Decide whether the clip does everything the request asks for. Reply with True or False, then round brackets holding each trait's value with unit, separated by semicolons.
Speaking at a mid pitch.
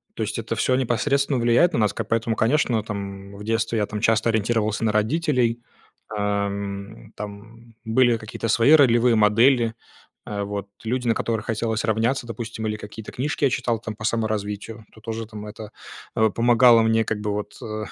False (110 Hz)